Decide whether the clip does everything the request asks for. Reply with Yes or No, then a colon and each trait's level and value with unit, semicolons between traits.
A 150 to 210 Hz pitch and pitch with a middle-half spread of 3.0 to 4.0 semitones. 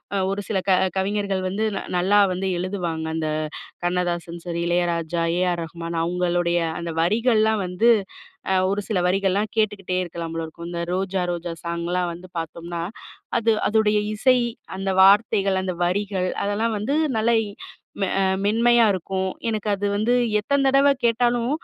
Yes: high, 190 Hz; average, 3.4 semitones